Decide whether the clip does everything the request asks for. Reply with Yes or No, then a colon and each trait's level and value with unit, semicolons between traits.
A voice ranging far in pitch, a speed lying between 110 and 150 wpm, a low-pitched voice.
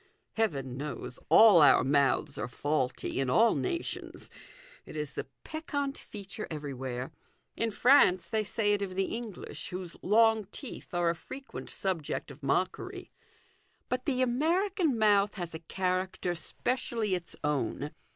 No: wide, 7.4 semitones; average, 140 wpm; high, 190 Hz